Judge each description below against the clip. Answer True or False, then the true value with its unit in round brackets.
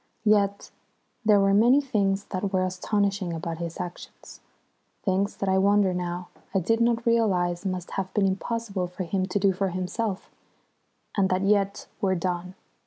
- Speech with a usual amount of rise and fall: False (2.0 semitones)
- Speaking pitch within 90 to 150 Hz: False (195 Hz)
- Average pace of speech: True (165 wpm)